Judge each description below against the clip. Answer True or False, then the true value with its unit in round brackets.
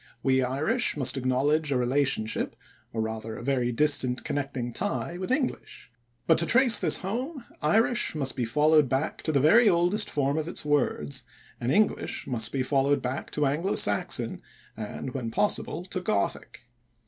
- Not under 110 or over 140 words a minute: False (165 wpm)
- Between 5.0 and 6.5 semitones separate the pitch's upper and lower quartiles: True (5.4 semitones)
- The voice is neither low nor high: True (145 Hz)